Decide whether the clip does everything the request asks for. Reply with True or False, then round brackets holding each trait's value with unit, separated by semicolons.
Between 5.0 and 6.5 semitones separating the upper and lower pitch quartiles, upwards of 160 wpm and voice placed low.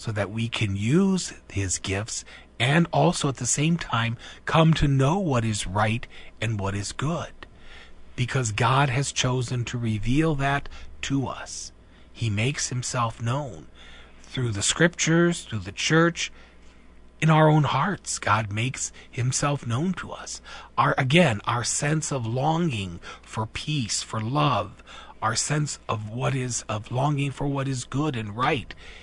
False (5.6 semitones; 155 wpm; 125 Hz)